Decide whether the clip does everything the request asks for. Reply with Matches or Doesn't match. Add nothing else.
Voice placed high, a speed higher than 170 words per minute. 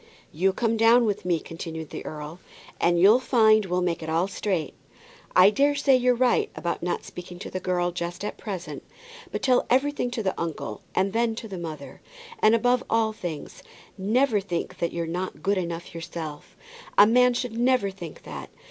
Matches